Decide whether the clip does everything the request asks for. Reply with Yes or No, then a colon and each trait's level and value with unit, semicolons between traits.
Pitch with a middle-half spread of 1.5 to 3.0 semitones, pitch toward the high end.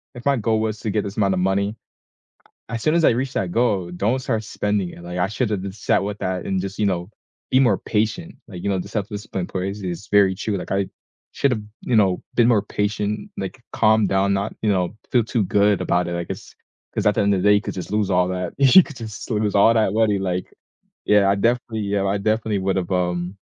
No: narrow, 2.6 semitones; low, 100 Hz